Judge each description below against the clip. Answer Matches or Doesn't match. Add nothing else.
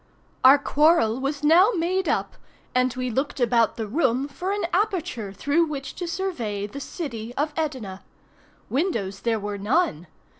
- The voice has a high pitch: Matches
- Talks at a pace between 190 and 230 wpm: Doesn't match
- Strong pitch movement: Matches